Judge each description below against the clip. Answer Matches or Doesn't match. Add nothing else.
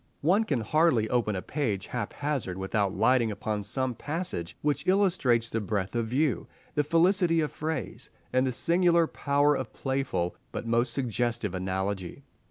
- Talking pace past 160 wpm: Doesn't match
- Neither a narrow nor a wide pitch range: Doesn't match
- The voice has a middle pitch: Doesn't match